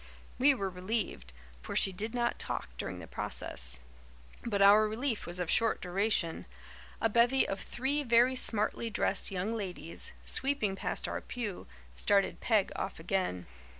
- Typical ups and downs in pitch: Yes, average, 4.0 semitones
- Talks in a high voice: Yes, high, 210 Hz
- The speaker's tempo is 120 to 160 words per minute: Yes, average, 150 wpm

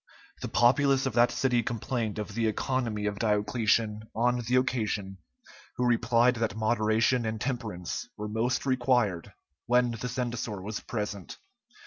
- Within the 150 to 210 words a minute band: No, average, 140 wpm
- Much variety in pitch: No, narrow, 2.6 semitones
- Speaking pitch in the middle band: No, low, 115 Hz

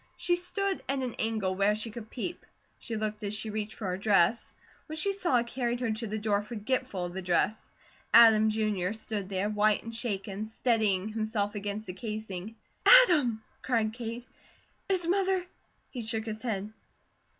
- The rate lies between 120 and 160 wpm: No, average, 175 wpm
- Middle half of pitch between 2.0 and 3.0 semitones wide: Yes, narrow, 2.6 semitones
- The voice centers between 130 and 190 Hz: No, high, 220 Hz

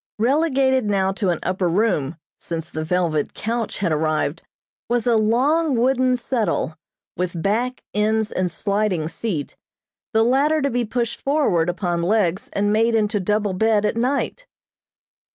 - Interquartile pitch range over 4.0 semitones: Yes, average, 5.2 semitones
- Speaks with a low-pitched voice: No, high, 215 Hz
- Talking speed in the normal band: Yes, average, 150 wpm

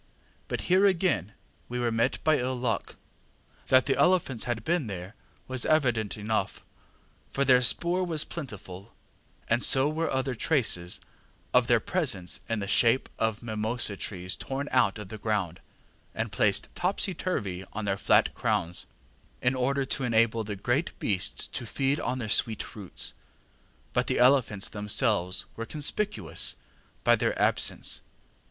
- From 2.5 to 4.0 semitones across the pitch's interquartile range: No, average, 4.8 semitones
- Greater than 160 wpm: No, average, 150 wpm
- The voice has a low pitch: Yes, low, 120 Hz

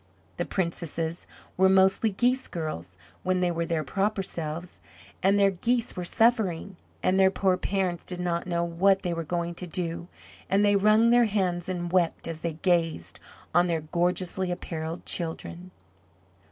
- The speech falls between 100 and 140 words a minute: No, average, 165 wpm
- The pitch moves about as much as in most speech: No, narrow, 2.3 semitones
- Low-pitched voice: No, medium, 180 Hz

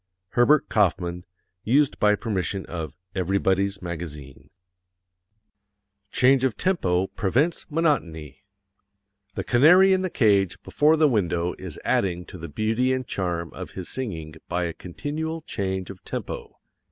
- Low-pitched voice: Yes, low, 100 Hz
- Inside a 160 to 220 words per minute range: No, slow, 135 wpm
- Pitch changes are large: Yes, wide, 7.1 semitones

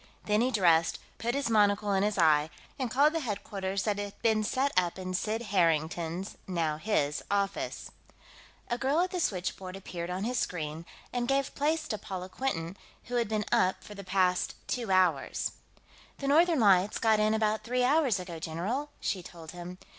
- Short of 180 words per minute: No, average, 185 wpm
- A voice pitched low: No, high, 200 Hz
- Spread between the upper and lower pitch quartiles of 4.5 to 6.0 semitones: Yes, average, 4.9 semitones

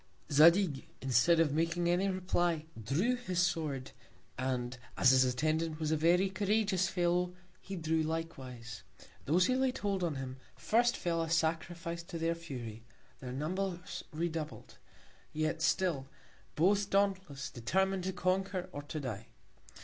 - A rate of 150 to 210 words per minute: No, average, 140 wpm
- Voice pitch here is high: No, medium, 165 Hz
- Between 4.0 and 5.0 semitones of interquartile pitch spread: Yes, average, 4.3 semitones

